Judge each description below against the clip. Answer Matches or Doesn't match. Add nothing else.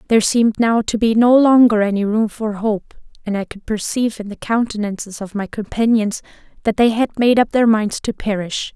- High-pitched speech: Matches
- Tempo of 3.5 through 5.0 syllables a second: Doesn't match